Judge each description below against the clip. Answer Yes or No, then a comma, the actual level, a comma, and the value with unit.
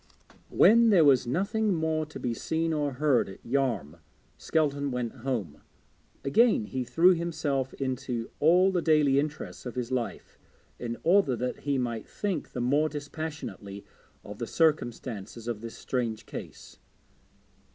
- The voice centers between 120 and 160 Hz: Yes, low, 135 Hz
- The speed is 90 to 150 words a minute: Yes, average, 145 wpm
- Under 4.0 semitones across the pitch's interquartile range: No, average, 4.9 semitones